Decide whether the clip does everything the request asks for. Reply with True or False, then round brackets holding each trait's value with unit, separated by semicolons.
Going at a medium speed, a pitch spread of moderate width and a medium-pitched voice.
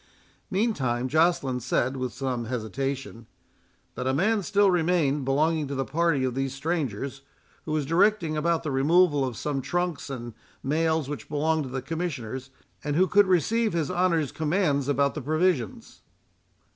True (160 wpm; 4.2 semitones; 150 Hz)